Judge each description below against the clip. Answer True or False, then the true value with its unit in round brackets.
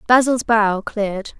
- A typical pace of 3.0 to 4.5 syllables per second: True (4.2 syllables/s)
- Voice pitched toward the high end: True (220 Hz)